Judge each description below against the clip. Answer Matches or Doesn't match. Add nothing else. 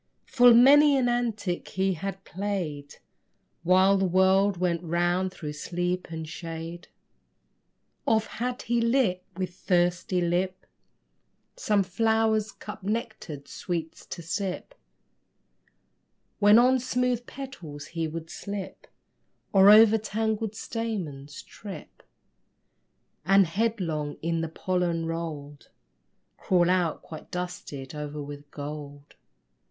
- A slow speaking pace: Matches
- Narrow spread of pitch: Doesn't match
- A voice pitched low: Doesn't match